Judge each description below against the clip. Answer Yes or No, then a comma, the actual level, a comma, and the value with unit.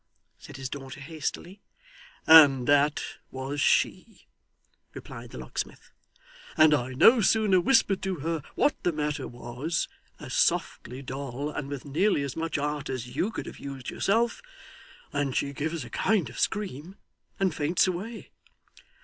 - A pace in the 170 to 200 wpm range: No, average, 150 wpm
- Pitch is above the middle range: No, medium, 150 Hz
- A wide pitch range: No, average, 4.8 semitones